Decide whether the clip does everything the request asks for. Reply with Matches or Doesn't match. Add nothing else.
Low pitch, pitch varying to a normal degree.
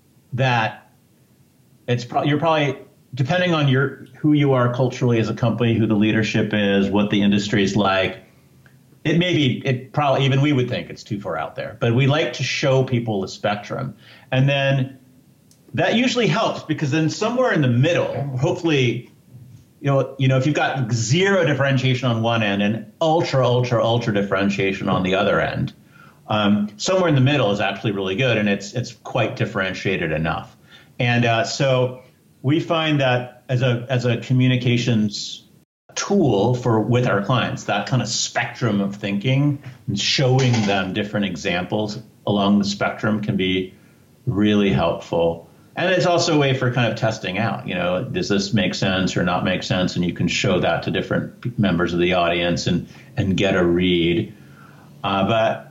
Matches